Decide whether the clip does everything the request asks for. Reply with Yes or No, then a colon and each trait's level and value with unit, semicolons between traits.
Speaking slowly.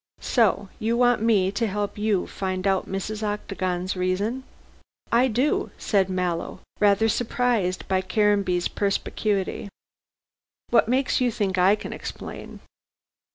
Yes: slow, 130 wpm